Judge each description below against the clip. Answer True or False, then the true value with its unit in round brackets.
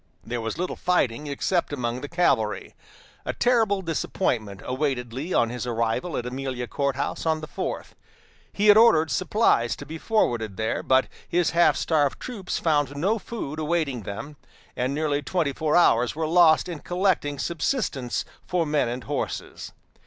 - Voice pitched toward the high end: False (150 Hz)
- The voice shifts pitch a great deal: True (6.0 semitones)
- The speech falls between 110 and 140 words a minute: False (165 wpm)